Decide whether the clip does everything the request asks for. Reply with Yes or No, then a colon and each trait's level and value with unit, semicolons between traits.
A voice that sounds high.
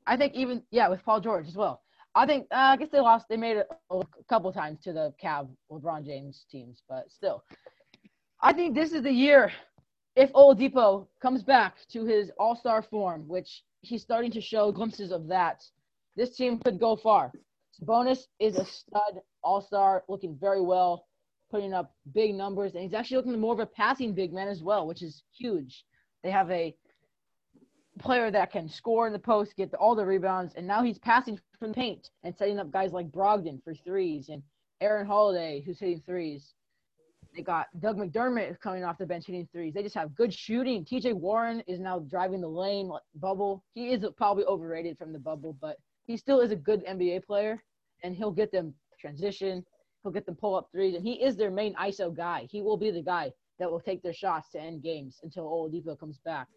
Yes: high, 200 Hz